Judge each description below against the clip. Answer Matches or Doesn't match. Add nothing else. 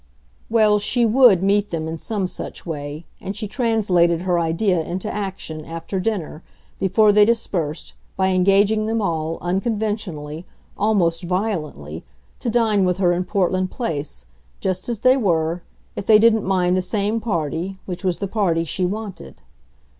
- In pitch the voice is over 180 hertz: Matches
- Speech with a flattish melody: Doesn't match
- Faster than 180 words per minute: Doesn't match